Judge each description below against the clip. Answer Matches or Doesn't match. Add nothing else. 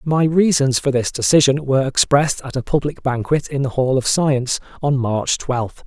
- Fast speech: Doesn't match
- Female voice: Doesn't match